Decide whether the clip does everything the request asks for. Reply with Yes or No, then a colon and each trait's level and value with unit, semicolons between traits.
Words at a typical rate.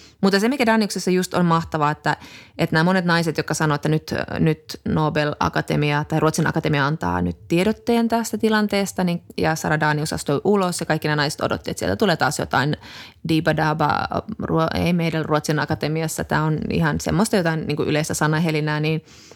No: fast, 175 wpm